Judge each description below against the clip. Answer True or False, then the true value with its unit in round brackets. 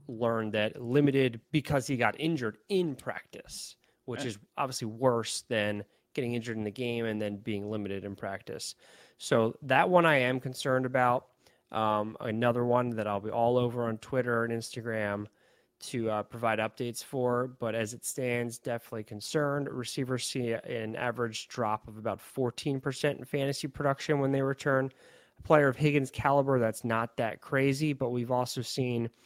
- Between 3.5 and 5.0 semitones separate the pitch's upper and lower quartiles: False (3.1 semitones)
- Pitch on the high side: False (120 Hz)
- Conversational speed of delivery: True (170 wpm)